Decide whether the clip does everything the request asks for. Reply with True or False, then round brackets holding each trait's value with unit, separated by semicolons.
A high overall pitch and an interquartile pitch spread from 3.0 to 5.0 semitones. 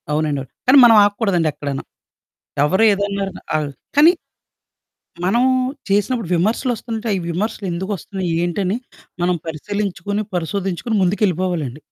True (195 Hz; 3.6 semitones)